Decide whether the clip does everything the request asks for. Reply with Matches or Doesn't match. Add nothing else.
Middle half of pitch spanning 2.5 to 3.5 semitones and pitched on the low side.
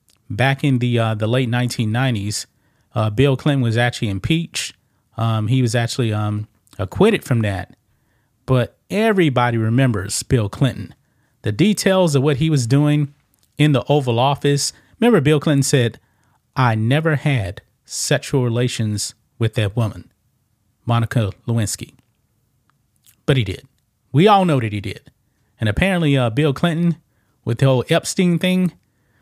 Doesn't match